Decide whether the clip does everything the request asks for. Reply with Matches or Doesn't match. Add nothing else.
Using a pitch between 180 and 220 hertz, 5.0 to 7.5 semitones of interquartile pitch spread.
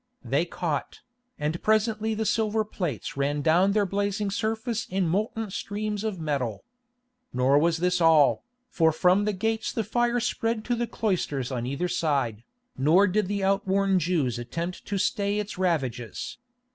Matches